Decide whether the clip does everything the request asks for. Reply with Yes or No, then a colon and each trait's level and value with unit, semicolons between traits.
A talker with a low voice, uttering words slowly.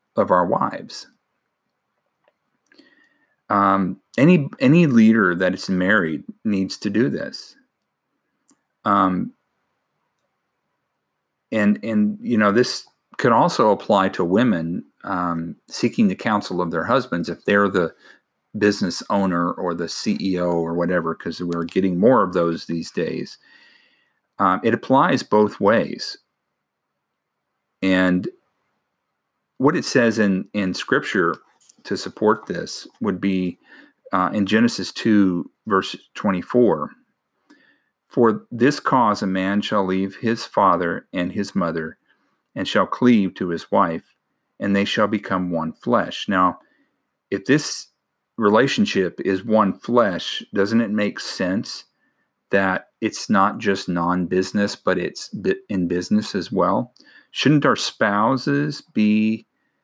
Yes: low, 100 Hz; slow, 125 wpm